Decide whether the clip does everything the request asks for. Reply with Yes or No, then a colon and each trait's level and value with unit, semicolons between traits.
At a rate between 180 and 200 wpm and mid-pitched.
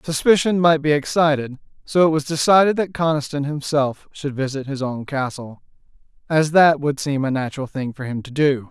Yes: average, 185 wpm; medium, 145 Hz